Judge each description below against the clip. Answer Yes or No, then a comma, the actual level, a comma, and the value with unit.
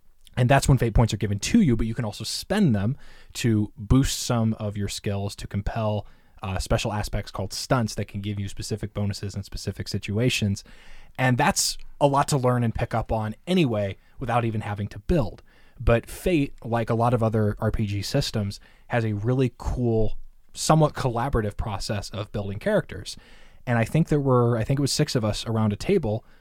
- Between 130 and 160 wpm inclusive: No, average, 200 wpm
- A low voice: Yes, low, 110 Hz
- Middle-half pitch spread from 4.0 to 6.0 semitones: No, average, 3.1 semitones